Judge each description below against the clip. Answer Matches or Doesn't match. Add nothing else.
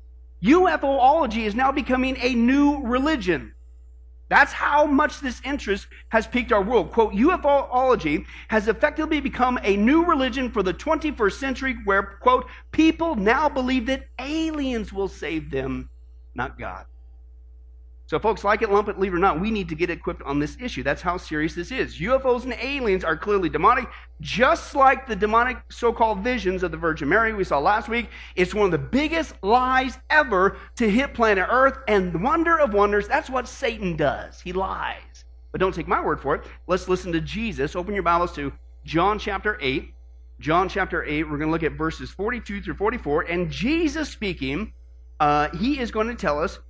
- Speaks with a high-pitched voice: Matches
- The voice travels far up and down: Matches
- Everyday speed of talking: Matches